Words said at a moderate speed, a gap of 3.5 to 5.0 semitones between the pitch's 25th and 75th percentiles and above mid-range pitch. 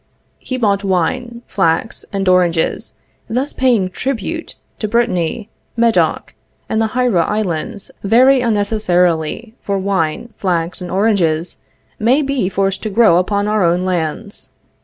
No: slow, 130 wpm; average, 4.4 semitones; high, 205 Hz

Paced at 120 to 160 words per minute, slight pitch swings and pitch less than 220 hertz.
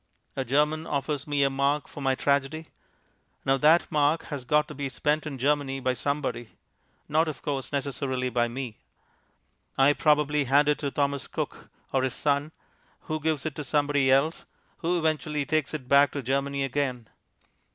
No: average, 170 wpm; narrow, 1.9 semitones; medium, 140 Hz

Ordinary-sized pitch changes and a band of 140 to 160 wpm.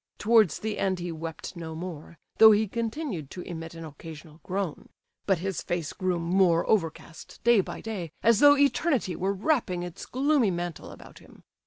No: average, 4.7 semitones; average, 175 wpm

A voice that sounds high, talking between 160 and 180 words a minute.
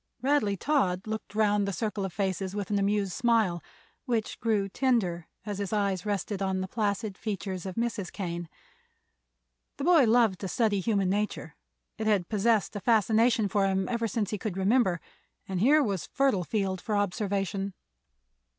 Yes: high, 205 Hz; average, 170 wpm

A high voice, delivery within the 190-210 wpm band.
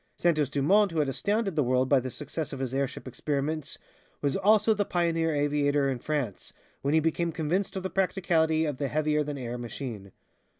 No: medium, 150 Hz; average, 195 wpm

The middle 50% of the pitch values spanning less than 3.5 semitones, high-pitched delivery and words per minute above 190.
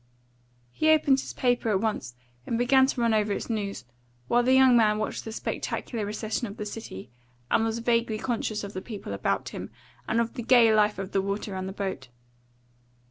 Yes: average, 2.7 semitones; high, 220 Hz; average, 200 wpm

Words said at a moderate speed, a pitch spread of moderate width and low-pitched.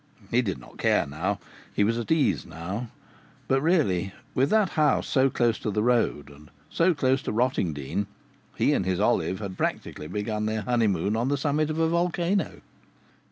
No: average, 180 wpm; wide, 6.8 semitones; low, 115 Hz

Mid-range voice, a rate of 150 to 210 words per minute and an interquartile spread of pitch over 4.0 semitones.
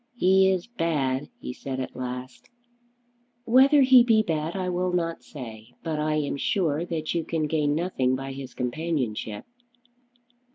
Yes: medium, 155 Hz; average, 155 wpm; wide, 5.5 semitones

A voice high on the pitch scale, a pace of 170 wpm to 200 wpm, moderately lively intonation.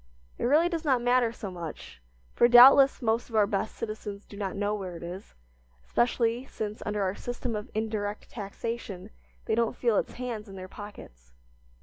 Yes: high, 215 Hz; average, 185 wpm; average, 3.2 semitones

